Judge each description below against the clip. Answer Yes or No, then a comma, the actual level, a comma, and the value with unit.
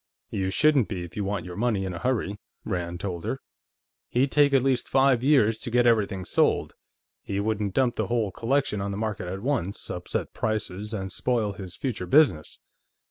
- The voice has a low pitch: Yes, low, 105 Hz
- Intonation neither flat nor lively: Yes, average, 4.4 semitones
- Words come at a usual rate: Yes, average, 190 wpm